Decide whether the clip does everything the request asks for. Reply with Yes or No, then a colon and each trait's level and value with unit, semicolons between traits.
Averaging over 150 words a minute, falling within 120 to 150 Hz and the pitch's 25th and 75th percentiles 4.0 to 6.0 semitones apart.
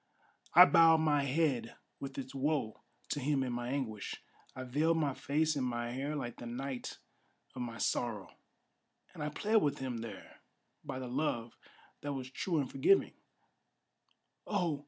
No: average, 160 wpm; low, 135 Hz; average, 3.6 semitones